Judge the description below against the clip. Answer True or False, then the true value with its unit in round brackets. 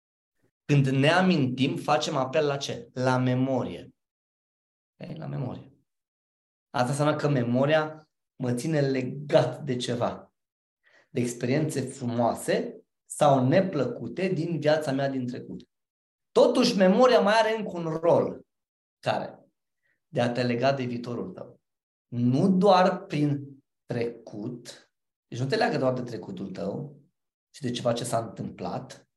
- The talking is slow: False (130 wpm)